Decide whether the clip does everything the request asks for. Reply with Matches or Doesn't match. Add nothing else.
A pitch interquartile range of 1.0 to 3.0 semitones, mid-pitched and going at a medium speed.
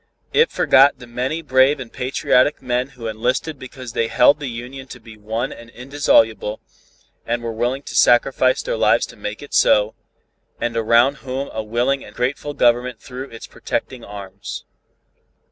Doesn't match